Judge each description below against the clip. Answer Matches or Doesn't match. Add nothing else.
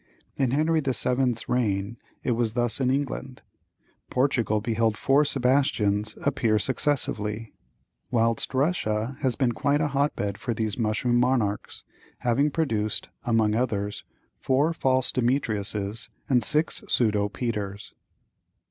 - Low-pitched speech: Matches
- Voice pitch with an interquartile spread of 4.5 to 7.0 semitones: Doesn't match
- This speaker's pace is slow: Matches